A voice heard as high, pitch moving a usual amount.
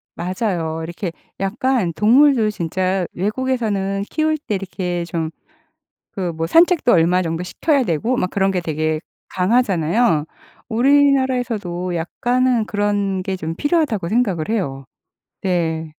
No: high, 195 Hz; wide, 5.9 semitones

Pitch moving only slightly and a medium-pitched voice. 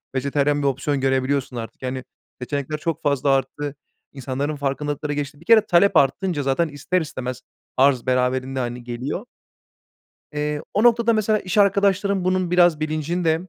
No: average, 4.7 semitones; medium, 145 Hz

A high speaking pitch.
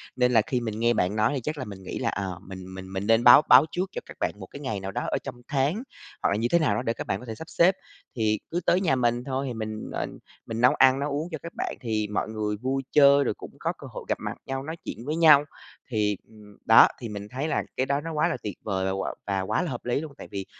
No: low, 120 Hz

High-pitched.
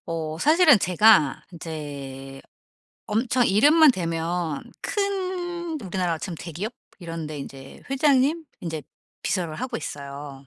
No: medium, 175 Hz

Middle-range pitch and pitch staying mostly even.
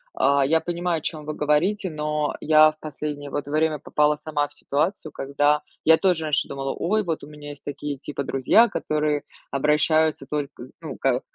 Yes: medium, 150 Hz; narrow, 1.6 semitones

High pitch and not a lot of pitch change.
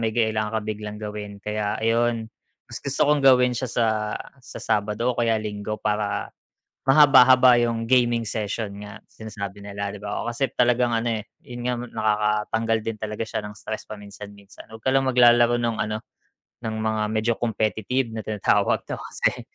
No: low, 110 Hz; narrow, 2.1 semitones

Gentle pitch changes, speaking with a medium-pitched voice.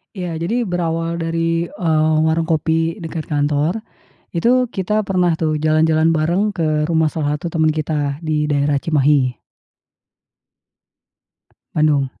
Yes: narrow, 1.8 semitones; medium, 160 Hz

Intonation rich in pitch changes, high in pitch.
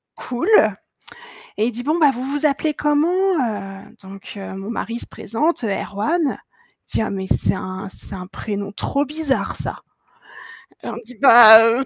Yes: wide, 6.5 semitones; high, 235 Hz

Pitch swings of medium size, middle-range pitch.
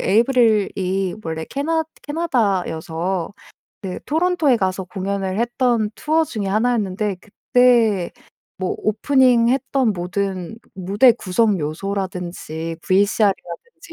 No: average, 4.8 semitones; high, 205 Hz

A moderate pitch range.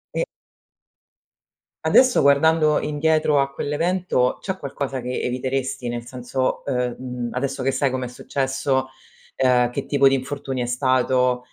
No: narrow, 2.2 semitones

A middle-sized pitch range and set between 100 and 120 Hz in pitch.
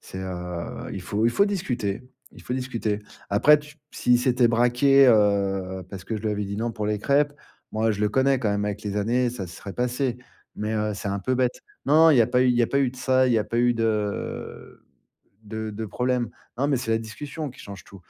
Yes: average, 3.7 semitones; low, 115 Hz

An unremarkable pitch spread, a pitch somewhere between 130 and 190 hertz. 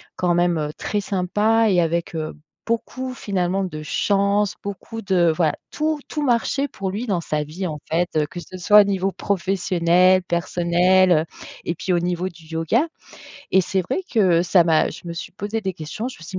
Yes: average, 3.0 semitones; medium, 185 Hz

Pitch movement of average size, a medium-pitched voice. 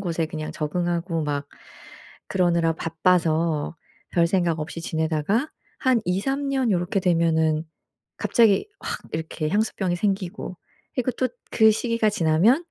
Yes: average, 4.8 semitones; medium, 175 Hz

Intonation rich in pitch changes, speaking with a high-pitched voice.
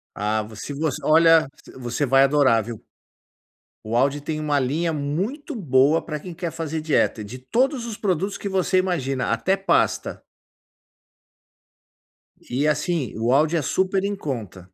No: wide, 5.7 semitones; medium, 150 Hz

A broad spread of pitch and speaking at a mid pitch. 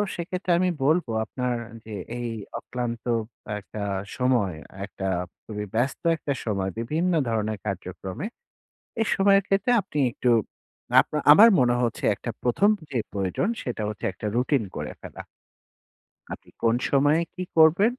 No: wide, 7.4 semitones; low, 125 Hz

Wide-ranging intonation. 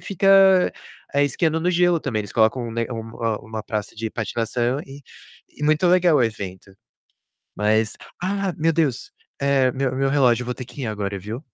Yes: wide, 6.2 semitones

